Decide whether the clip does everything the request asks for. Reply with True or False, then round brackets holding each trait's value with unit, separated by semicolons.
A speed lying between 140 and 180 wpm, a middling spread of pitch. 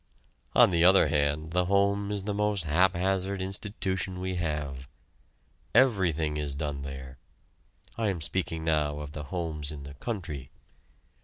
True (145 wpm; 4.5 semitones)